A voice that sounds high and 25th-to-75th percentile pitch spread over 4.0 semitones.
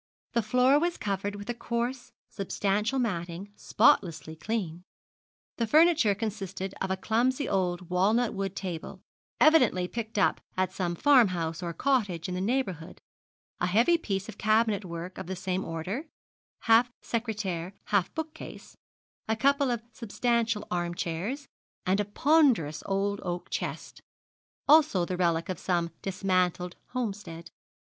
Yes: high, 200 Hz; average, 4.7 semitones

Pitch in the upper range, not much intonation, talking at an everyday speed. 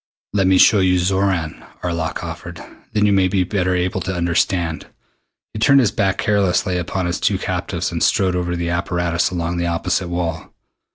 No: very low, 90 Hz; narrow, 1.8 semitones; average, 185 wpm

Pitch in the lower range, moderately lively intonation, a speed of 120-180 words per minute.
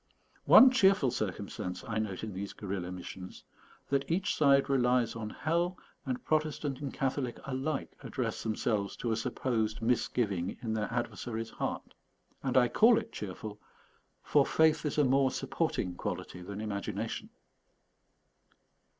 Yes: low, 120 Hz; average, 4.7 semitones; average, 140 wpm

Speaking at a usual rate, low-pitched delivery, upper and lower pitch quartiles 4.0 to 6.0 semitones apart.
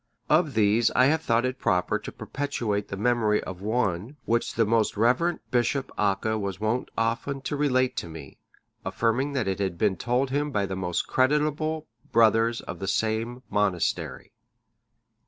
Yes: average, 160 wpm; low, 115 Hz; average, 4.3 semitones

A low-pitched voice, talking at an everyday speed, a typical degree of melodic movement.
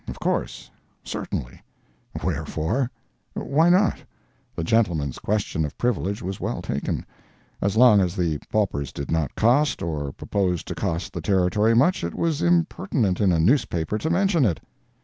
No: low, 100 Hz; average, 150 wpm; wide, 7.5 semitones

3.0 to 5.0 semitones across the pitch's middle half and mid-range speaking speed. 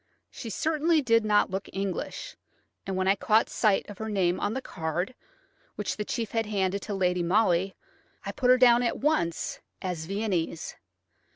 Yes: average, 3.7 semitones; average, 175 wpm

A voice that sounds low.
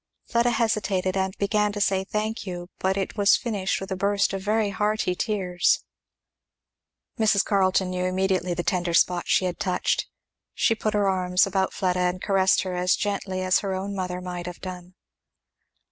No: high, 190 Hz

